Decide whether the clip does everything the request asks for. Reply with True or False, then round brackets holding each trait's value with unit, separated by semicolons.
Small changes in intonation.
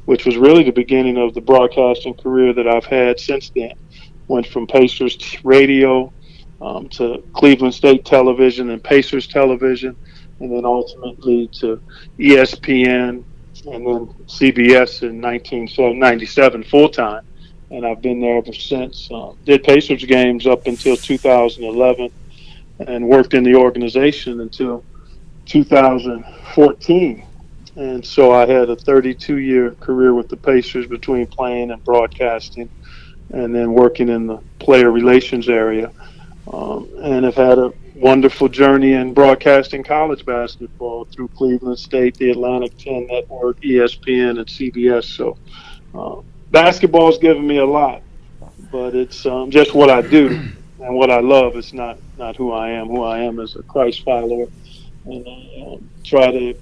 True (1.8 semitones)